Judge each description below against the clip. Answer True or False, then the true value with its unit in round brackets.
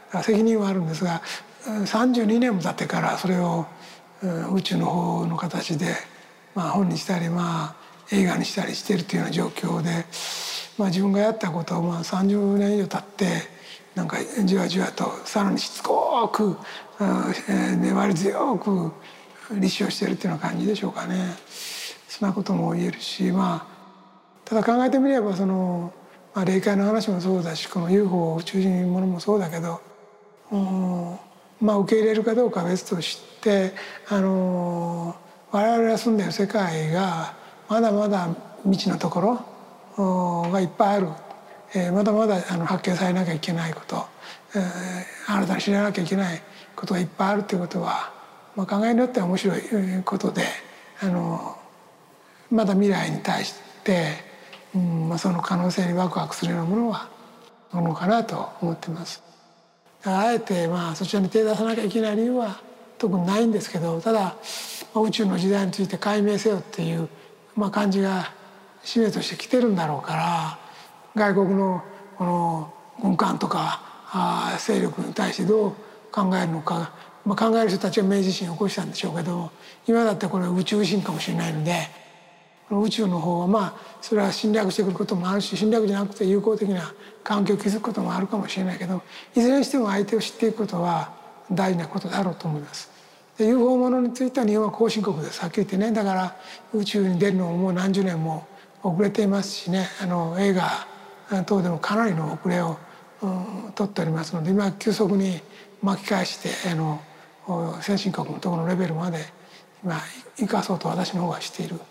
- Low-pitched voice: False (195 Hz)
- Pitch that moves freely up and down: False (3.0 semitones)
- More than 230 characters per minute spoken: True (345 characters per minute)